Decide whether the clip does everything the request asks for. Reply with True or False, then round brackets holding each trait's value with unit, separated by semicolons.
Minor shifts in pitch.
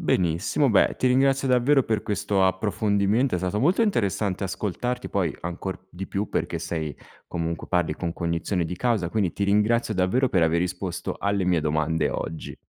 False (4.5 semitones)